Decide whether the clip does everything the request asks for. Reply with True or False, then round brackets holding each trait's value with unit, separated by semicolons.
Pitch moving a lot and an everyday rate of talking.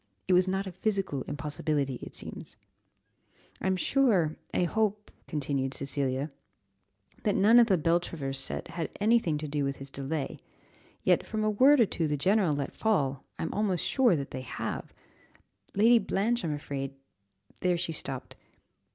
True (6.5 semitones; 165 wpm)